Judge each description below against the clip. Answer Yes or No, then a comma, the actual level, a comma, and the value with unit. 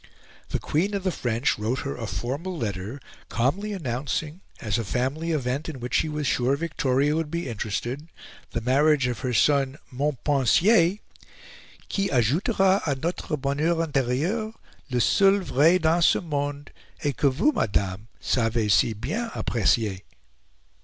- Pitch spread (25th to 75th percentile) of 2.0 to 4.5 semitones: No, average, 5.2 semitones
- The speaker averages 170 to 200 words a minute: No, average, 145 wpm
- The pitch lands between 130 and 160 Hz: Yes, medium, 140 Hz